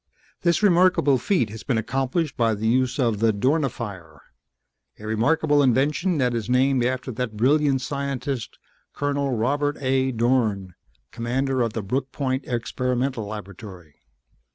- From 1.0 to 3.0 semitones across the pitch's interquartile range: No, average, 3.7 semitones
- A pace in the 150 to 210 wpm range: No, slow, 135 wpm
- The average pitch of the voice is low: Yes, low, 130 Hz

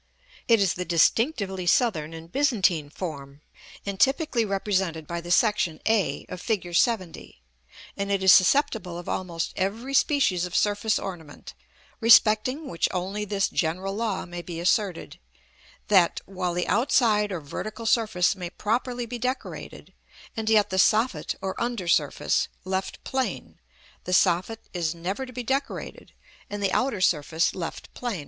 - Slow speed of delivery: No, average, 150 wpm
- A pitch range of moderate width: Yes, average, 4.4 semitones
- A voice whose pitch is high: Yes, high, 195 Hz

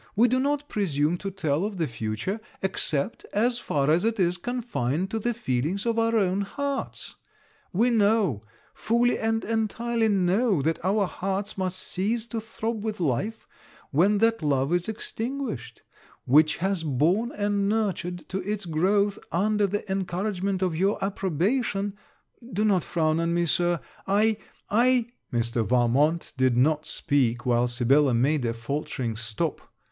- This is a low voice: No, high, 190 Hz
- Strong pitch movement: Yes, wide, 6.4 semitones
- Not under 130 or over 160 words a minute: Yes, average, 155 wpm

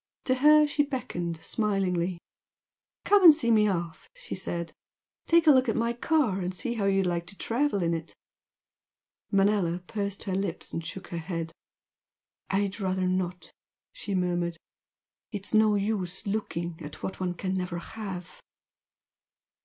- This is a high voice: Yes, high, 195 Hz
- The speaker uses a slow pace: No, average, 155 wpm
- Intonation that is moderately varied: Yes, average, 3.9 semitones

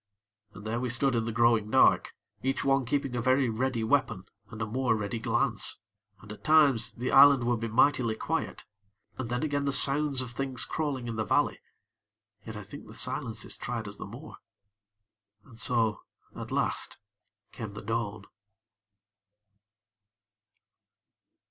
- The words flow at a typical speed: Yes, average, 155 wpm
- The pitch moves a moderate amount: Yes, average, 3.2 semitones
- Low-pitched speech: Yes, low, 120 Hz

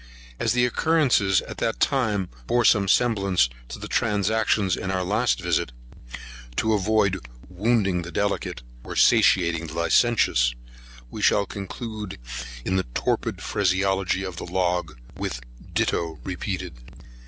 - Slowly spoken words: Yes, slow, 130 wpm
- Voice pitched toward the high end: No, very low, 95 Hz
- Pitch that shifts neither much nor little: Yes, average, 3.3 semitones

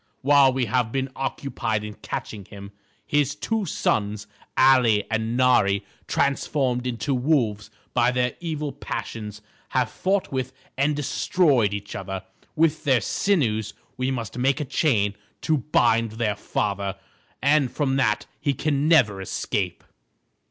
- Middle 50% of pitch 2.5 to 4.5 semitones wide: No, average, 4.9 semitones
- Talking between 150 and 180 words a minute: No, average, 140 wpm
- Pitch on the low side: Yes, low, 125 Hz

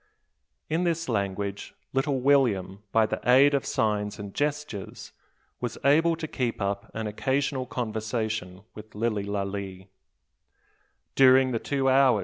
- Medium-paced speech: No, slow, 115 wpm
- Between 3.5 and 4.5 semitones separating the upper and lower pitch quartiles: No, average, 5.3 semitones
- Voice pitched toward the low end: Yes, low, 110 Hz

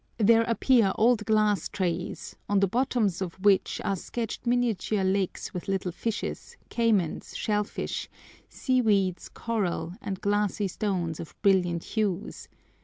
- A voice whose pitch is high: Yes, high, 205 Hz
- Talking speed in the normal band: No, slow, 130 wpm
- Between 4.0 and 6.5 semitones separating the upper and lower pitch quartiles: No, average, 3.0 semitones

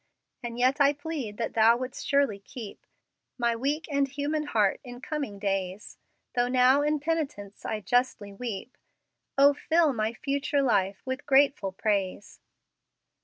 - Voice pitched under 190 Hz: No, very high, 250 Hz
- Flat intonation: No, average, 5.1 semitones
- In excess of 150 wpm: No, average, 145 wpm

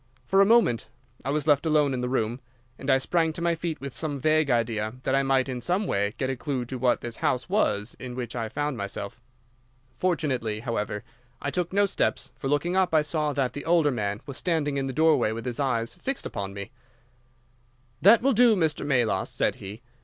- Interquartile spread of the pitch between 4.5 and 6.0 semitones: Yes, average, 5.2 semitones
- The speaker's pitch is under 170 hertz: Yes, low, 135 Hz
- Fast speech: Yes, fast, 215 wpm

